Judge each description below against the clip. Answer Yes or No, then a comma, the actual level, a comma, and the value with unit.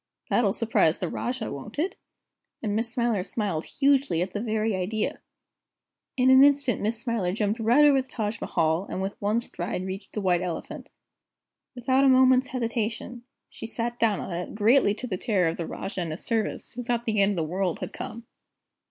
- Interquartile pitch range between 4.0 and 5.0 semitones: Yes, average, 4.4 semitones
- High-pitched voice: Yes, high, 220 Hz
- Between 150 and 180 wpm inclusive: No, average, 195 wpm